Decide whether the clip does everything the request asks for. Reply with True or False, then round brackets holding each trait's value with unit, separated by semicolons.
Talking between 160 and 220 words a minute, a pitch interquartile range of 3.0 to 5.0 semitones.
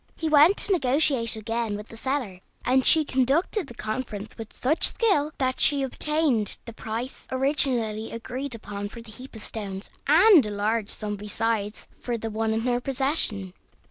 True (175 wpm; 4.3 semitones)